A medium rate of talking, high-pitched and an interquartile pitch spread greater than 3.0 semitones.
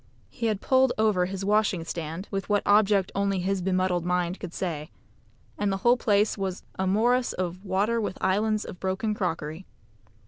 No: average, 175 wpm; high, 195 Hz; narrow, 2.6 semitones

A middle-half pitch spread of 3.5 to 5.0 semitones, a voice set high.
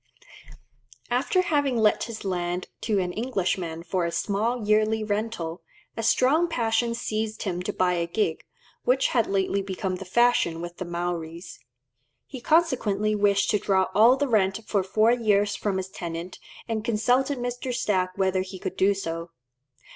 Yes: average, 4.1 semitones; high, 205 Hz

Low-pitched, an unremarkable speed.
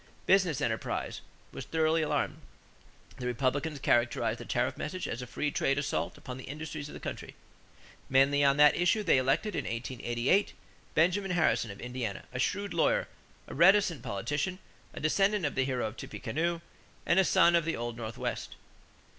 No: medium, 145 Hz; average, 170 wpm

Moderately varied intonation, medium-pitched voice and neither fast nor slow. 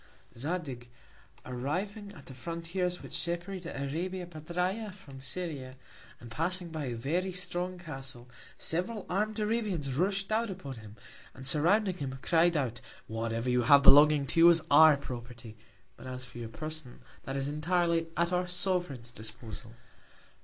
No: wide, 5.7 semitones; medium, 160 Hz; average, 150 wpm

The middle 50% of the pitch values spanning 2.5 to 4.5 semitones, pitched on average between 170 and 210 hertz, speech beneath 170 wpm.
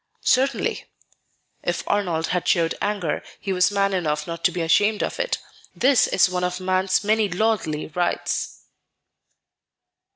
Yes: average, 3.3 semitones; medium, 185 Hz; average, 140 wpm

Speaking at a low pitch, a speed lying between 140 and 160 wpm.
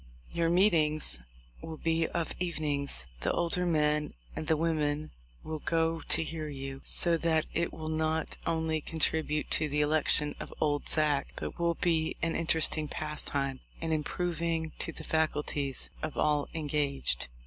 No: medium, 155 Hz; average, 150 wpm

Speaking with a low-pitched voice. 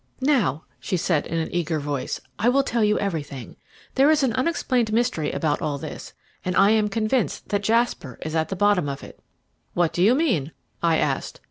No: high, 195 Hz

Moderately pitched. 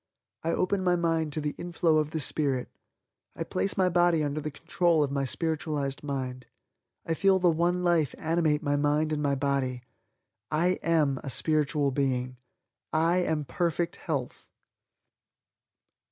Yes: medium, 155 Hz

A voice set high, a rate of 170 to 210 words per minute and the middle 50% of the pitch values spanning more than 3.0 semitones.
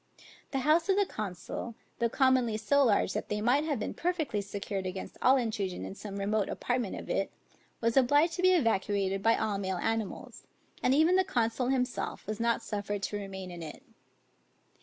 Yes: high, 225 Hz; average, 185 wpm; average, 5.0 semitones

